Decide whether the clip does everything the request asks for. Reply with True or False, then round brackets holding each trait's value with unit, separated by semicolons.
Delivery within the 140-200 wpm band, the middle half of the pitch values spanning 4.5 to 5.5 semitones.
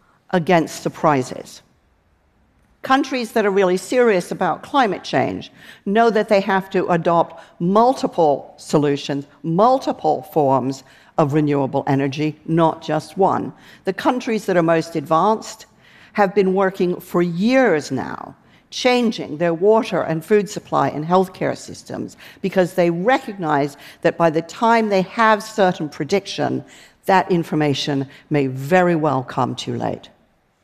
False (130 wpm; 5.2 semitones)